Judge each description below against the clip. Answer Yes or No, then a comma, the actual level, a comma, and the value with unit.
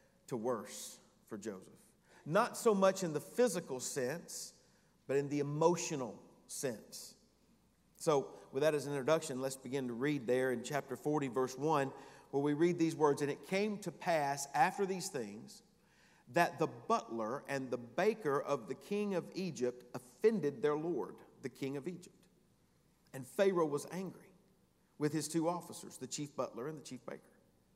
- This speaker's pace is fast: No, average, 170 wpm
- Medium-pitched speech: Yes, medium, 150 Hz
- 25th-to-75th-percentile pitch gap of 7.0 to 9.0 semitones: No, average, 4.4 semitones